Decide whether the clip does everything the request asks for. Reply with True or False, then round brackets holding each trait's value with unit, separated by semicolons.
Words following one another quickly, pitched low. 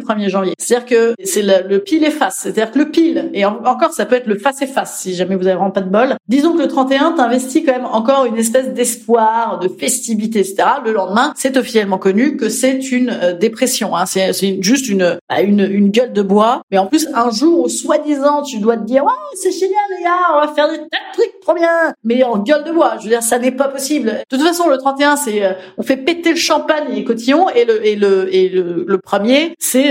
False (250 wpm; 250 Hz)